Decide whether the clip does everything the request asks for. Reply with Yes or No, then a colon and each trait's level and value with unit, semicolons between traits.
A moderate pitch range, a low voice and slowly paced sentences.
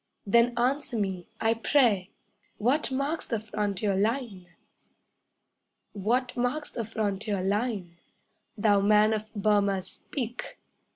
No: average, 3.3 semitones; high, 215 Hz; slow, 110 wpm